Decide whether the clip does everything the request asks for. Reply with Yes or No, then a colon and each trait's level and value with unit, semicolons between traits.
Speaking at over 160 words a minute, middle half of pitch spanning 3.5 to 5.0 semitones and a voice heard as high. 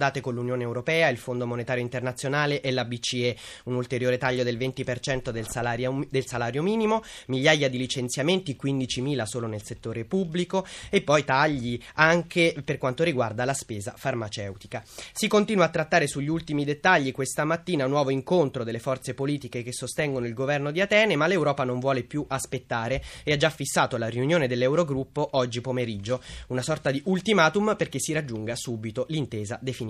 No: fast, 170 wpm; average, 3.8 semitones; low, 135 Hz